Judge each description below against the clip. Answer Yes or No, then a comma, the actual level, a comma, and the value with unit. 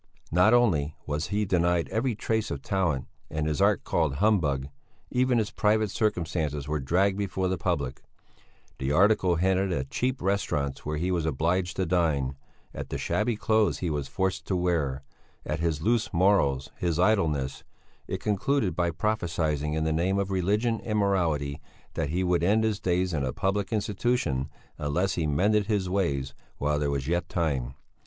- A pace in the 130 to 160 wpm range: No, average, 175 wpm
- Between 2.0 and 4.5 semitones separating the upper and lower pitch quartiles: No, average, 5.1 semitones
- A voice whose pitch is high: No, very low, 90 Hz